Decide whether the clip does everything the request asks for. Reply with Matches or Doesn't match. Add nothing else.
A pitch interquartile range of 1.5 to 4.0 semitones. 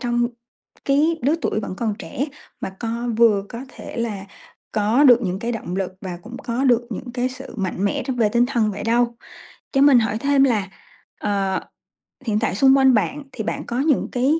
Matches